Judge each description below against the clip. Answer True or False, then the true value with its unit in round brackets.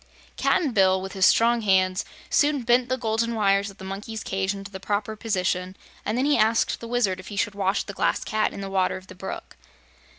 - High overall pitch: True (200 Hz)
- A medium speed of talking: False (225 wpm)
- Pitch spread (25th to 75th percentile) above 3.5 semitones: False (3.1 semitones)